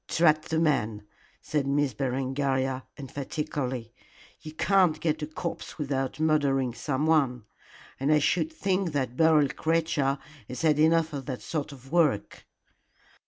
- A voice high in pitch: No, medium, 145 Hz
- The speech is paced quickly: No, slow, 135 wpm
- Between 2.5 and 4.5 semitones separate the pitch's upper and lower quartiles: Yes, average, 3.0 semitones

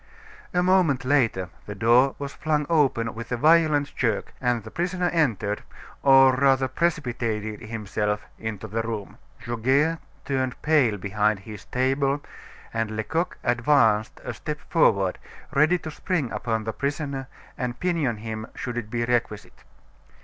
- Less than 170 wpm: Yes, average, 140 wpm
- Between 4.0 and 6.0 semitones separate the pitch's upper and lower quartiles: Yes, average, 4.9 semitones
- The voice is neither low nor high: No, low, 125 Hz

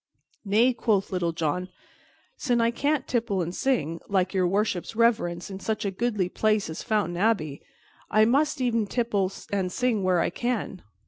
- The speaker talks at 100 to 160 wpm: No, average, 170 wpm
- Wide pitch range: No, average, 4.3 semitones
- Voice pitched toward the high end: Yes, high, 210 Hz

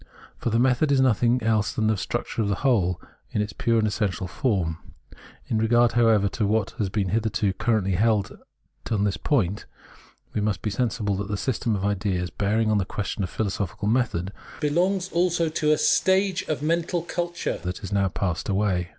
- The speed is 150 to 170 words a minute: No, average, 190 wpm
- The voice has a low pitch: Yes, low, 110 Hz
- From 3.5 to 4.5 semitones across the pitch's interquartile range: Yes, average, 4.0 semitones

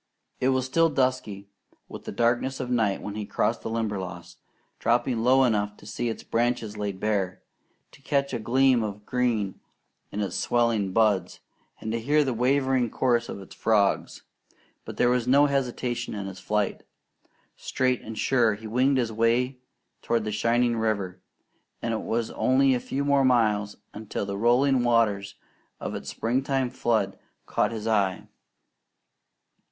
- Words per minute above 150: Yes, average, 160 wpm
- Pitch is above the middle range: No, low, 115 Hz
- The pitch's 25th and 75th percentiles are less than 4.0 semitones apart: Yes, average, 3.4 semitones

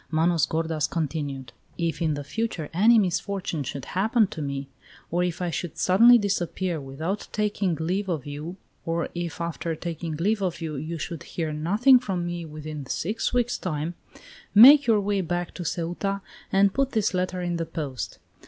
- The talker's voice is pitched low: No, medium, 175 Hz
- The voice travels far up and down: No, average, 3.9 semitones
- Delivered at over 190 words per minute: No, average, 175 wpm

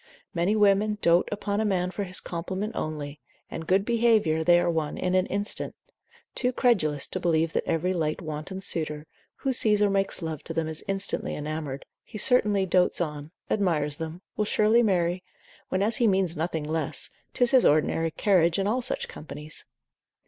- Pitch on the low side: No, medium, 180 Hz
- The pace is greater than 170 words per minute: Yes, average, 180 wpm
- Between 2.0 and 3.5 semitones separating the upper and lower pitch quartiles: No, average, 4.3 semitones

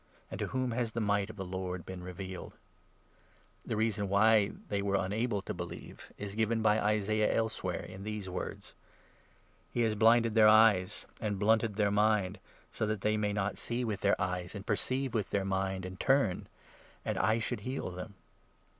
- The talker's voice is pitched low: Yes, low, 105 Hz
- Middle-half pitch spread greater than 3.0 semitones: No, narrow, 2.4 semitones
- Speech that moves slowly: No, average, 200 wpm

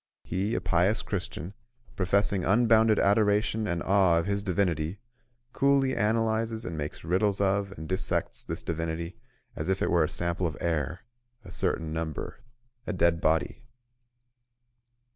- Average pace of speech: Yes, average, 145 wpm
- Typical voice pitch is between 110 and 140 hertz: No, very low, 95 Hz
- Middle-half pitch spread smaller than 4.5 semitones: Yes, average, 3.9 semitones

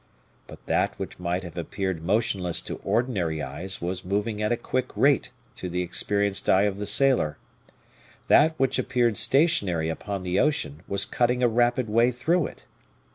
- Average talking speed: Yes, average, 170 wpm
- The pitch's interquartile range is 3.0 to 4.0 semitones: No, wide, 5.4 semitones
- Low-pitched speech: Yes, low, 105 Hz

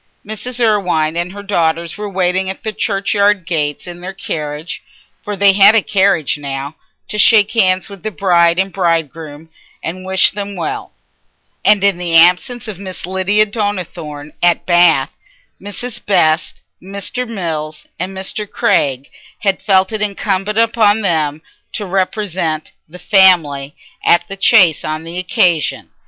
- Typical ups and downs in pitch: Yes, average, 3.6 semitones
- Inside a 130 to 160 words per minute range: Yes, average, 150 wpm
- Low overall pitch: No, medium, 185 Hz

